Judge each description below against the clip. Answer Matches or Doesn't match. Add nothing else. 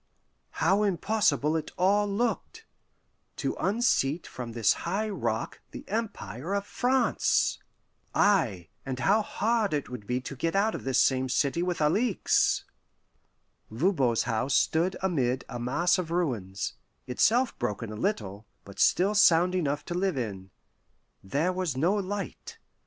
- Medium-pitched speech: Matches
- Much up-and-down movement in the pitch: Matches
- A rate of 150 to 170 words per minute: Doesn't match